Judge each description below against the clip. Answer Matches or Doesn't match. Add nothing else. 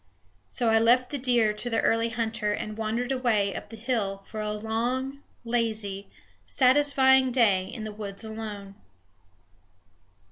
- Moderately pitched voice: Doesn't match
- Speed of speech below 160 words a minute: Matches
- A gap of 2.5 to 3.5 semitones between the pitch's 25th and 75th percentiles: Matches